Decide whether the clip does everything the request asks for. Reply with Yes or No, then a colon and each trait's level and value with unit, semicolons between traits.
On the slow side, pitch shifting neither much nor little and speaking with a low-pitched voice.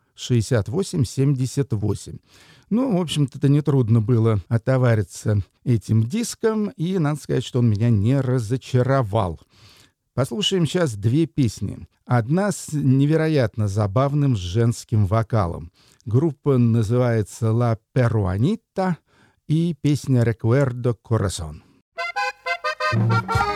Yes: slow, 90 wpm; average, 4.6 semitones; low, 125 Hz